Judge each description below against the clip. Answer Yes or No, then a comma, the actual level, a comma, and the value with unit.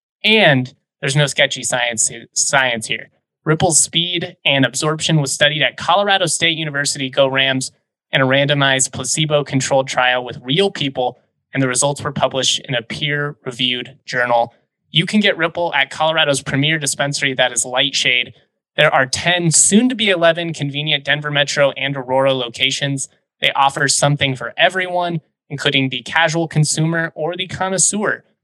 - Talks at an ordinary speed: Yes, average, 155 wpm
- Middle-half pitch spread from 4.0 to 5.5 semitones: No, average, 3.5 semitones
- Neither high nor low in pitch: Yes, medium, 145 Hz